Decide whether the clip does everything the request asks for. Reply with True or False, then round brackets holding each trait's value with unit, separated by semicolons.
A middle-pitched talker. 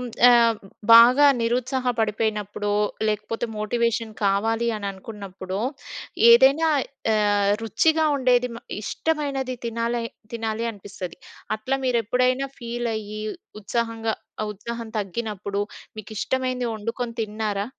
False (230 Hz)